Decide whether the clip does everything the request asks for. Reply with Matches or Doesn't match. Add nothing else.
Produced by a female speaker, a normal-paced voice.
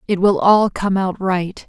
Doesn't match